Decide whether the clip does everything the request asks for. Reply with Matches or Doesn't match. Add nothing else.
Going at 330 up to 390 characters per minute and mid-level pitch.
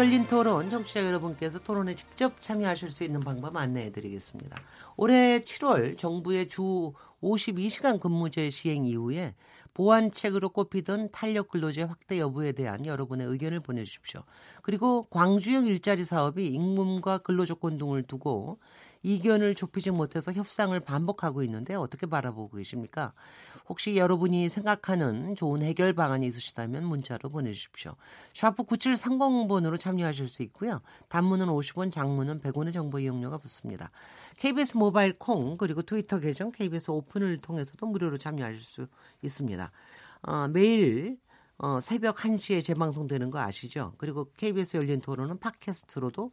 Matches